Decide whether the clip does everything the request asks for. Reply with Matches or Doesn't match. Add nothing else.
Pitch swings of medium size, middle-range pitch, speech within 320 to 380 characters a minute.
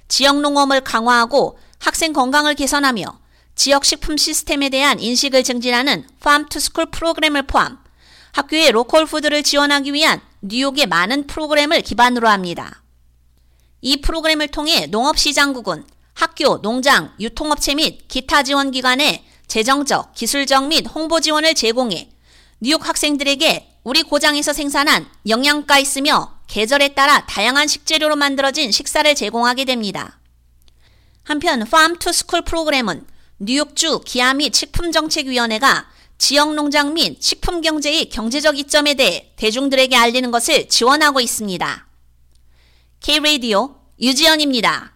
Doesn't match